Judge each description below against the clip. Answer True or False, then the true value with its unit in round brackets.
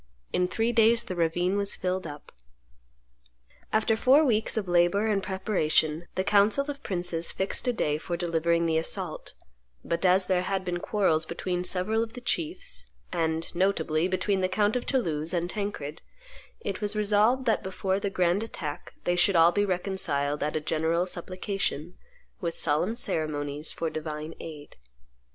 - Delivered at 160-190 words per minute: True (165 wpm)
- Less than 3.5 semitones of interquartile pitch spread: False (3.9 semitones)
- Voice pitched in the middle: True (180 Hz)